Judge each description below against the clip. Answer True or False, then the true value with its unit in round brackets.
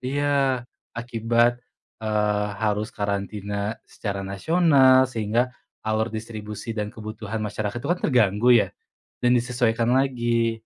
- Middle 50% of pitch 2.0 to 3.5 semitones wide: True (2.7 semitones)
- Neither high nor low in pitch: False (115 Hz)